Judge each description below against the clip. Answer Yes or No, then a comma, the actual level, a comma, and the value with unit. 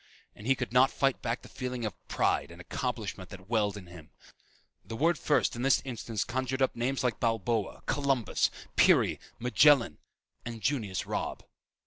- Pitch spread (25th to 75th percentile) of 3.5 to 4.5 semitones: Yes, average, 3.9 semitones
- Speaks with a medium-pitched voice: No, low, 120 Hz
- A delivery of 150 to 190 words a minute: Yes, average, 165 wpm